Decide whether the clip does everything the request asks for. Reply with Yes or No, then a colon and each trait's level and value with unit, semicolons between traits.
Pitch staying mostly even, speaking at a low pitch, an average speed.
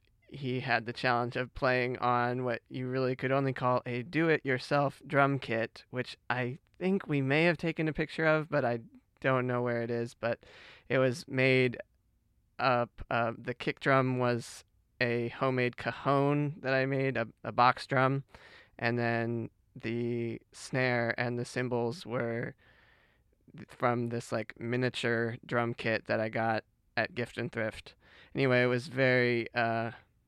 Yes: narrow, 2.1 semitones; low, 125 Hz; average, 160 wpm